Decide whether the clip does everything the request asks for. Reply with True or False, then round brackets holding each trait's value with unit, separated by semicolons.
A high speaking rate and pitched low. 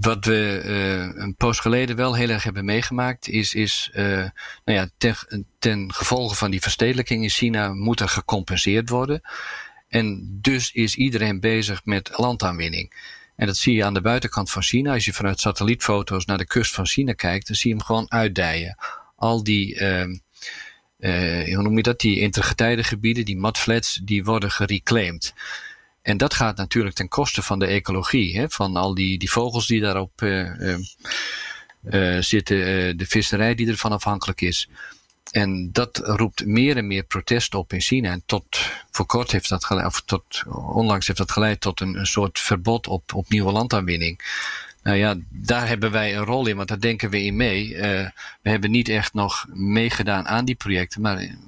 False (185 wpm; 105 Hz)